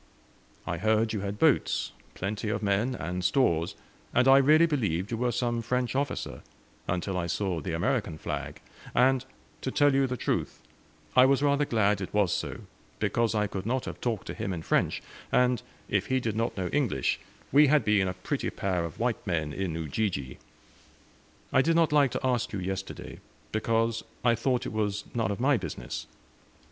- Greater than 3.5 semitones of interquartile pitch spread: Yes, average, 5.1 semitones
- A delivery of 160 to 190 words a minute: Yes, average, 185 wpm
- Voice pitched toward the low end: Yes, low, 110 Hz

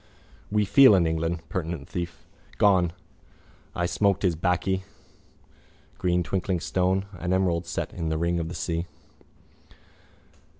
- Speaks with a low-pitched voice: Yes, very low, 90 Hz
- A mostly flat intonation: Yes, narrow, 2.1 semitones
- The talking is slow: Yes, slow, 130 wpm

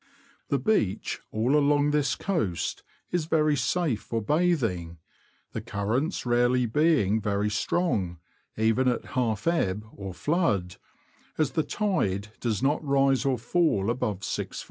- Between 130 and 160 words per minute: Yes, slow, 135 wpm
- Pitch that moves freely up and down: Yes, wide, 6.4 semitones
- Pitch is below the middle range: Yes, low, 125 Hz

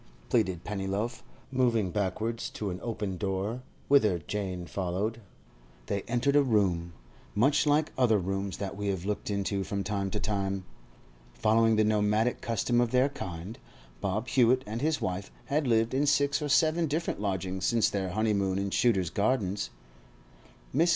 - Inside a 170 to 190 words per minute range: No, average, 155 wpm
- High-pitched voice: No, low, 105 Hz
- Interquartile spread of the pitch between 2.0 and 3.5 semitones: No, average, 4.0 semitones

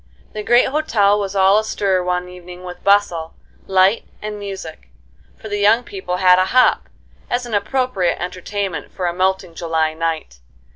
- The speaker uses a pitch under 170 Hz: No, high, 190 Hz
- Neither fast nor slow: Yes, average, 160 wpm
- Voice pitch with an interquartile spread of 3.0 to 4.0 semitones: No, narrow, 2.5 semitones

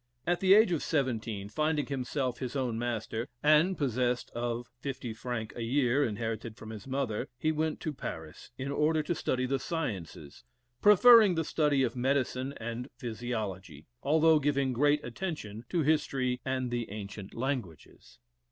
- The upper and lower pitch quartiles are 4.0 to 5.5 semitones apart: Yes, average, 4.5 semitones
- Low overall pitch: Yes, low, 130 Hz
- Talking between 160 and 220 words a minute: No, average, 150 wpm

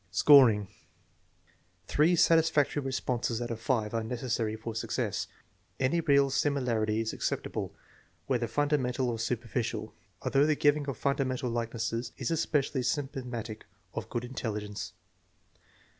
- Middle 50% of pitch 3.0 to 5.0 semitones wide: Yes, average, 3.7 semitones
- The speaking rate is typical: No, slow, 130 wpm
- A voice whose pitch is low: Yes, low, 125 Hz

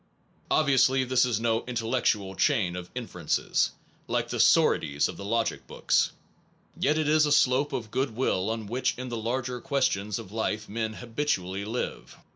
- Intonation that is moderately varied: Yes, average, 3.7 semitones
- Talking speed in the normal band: Yes, average, 170 wpm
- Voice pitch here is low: Yes, low, 115 Hz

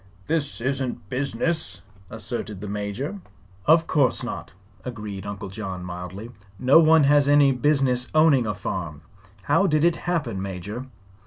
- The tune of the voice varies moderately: No, wide, 6.4 semitones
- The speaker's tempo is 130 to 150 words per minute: Yes, average, 140 wpm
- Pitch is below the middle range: Yes, low, 125 Hz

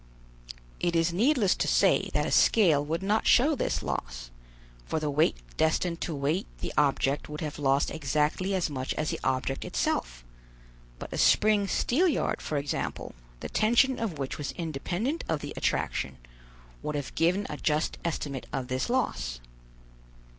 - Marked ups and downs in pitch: Yes, wide, 5.9 semitones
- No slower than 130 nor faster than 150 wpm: No, average, 160 wpm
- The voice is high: No, medium, 155 Hz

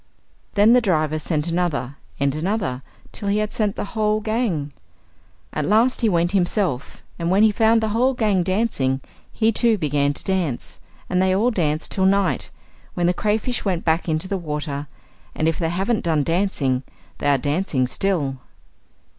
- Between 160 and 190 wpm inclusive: Yes, average, 180 wpm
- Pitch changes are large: Yes, wide, 5.7 semitones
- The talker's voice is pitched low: No, medium, 180 Hz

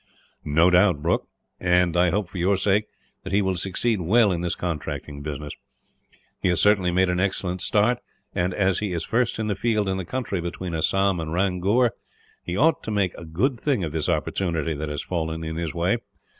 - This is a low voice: Yes, very low, 90 Hz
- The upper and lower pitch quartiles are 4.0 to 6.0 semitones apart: No, average, 3.3 semitones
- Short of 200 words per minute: No, fast, 205 wpm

